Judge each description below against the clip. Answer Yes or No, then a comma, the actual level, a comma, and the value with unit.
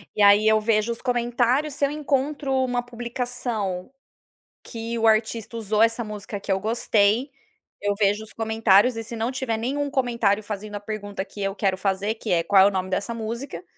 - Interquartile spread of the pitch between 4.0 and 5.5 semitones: No, average, 2.9 semitones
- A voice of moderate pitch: No, high, 220 Hz